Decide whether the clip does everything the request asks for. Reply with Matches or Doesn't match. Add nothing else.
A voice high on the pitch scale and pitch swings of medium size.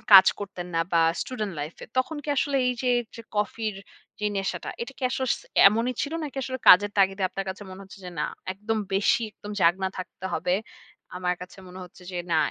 Matches